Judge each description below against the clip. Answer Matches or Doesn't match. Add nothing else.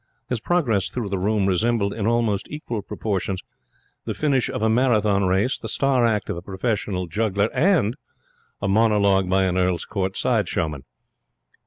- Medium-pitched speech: Doesn't match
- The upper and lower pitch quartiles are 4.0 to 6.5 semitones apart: Doesn't match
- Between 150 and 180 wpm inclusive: Matches